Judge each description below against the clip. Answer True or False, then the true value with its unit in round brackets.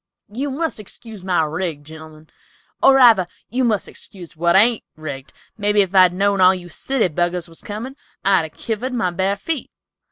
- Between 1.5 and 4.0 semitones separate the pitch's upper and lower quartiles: False (4.8 semitones)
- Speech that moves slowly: False (180 wpm)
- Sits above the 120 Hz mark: True (190 Hz)